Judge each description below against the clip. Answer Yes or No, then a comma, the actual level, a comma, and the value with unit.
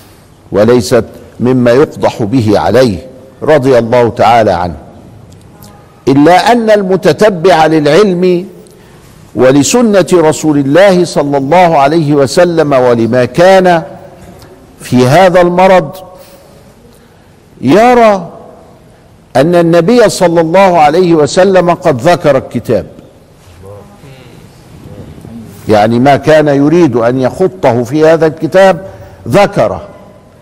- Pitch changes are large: Yes, wide, 6.5 semitones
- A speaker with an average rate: Yes, average, 90 wpm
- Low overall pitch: No, medium, 160 Hz